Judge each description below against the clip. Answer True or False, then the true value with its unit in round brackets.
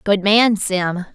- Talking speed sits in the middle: True (155 wpm)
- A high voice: True (200 Hz)